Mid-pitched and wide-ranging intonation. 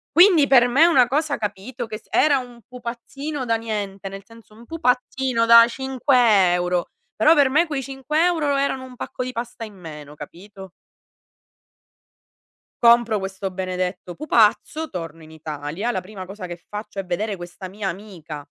No: high, 225 Hz; wide, 5.7 semitones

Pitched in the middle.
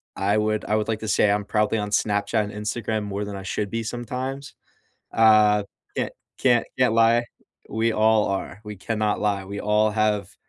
No: low, 105 Hz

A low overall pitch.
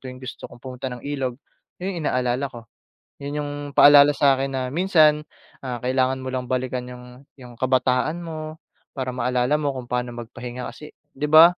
Yes: low, 130 Hz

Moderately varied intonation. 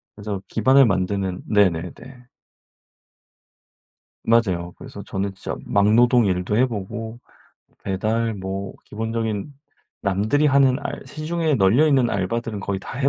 Yes: average, 3.9 semitones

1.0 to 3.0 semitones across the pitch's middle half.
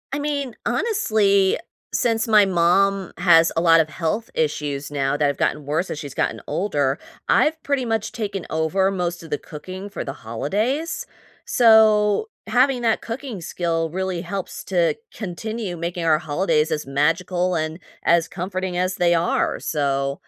No: average, 4.9 semitones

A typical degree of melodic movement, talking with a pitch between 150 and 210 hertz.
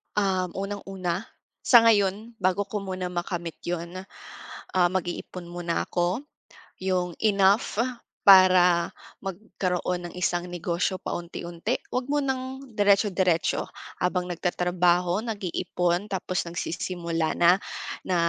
No: narrow, 2.3 semitones; medium, 185 Hz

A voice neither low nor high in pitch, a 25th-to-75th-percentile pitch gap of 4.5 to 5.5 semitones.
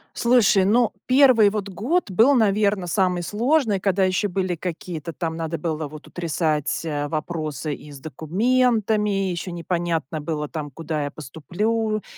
Yes: medium, 180 Hz; average, 5.1 semitones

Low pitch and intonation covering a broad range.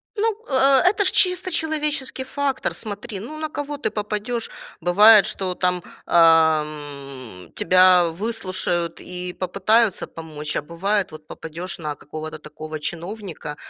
No: medium, 185 Hz; wide, 6.9 semitones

